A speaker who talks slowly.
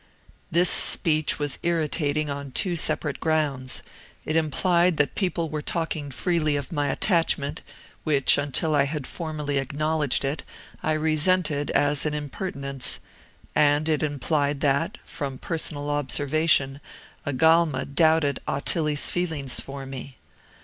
Yes: slow, 125 wpm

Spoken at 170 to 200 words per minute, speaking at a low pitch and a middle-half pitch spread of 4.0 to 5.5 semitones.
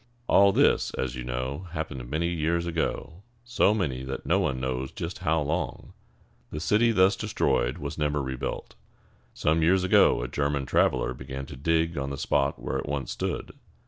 Yes: average, 175 wpm; very low, 75 Hz; average, 4.4 semitones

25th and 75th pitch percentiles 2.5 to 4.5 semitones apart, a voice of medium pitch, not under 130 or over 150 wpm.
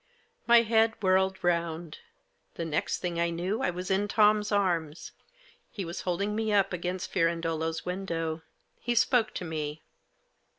Yes: average, 3.6 semitones; medium, 180 Hz; average, 145 wpm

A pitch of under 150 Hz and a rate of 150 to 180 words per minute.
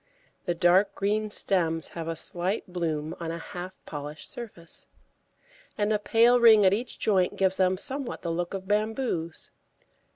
No: medium, 185 Hz; average, 160 wpm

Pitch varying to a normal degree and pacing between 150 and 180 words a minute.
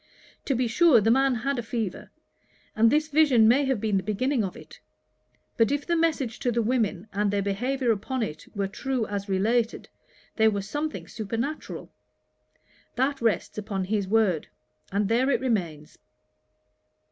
Yes: average, 4.5 semitones; average, 165 wpm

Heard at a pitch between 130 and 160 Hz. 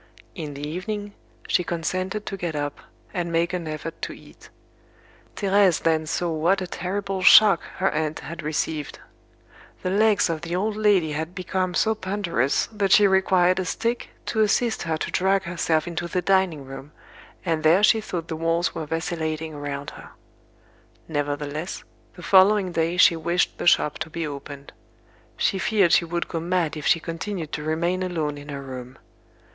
No: medium, 170 Hz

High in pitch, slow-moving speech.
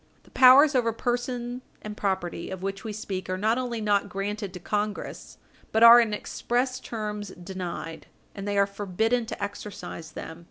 No: high, 210 Hz; average, 170 wpm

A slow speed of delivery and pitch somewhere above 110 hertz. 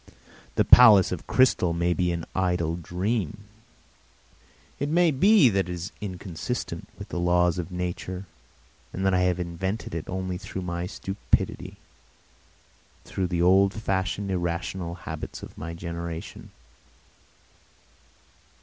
No: slow, 130 wpm; very low, 90 Hz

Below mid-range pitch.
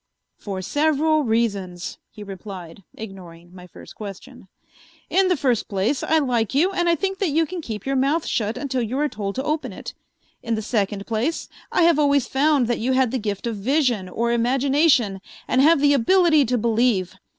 No: high, 245 Hz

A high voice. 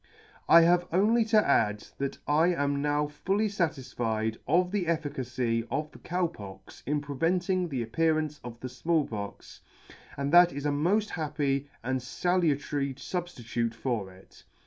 No: medium, 145 Hz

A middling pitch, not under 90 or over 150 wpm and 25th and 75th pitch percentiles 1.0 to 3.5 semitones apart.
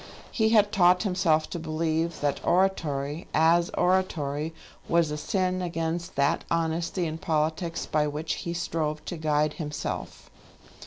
Yes: medium, 165 Hz; average, 140 wpm; narrow, 2.5 semitones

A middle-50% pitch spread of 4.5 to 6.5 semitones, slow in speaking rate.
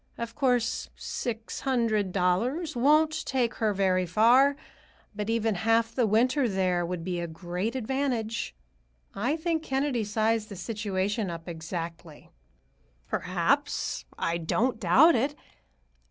Yes: wide, 5.6 semitones; slow, 125 wpm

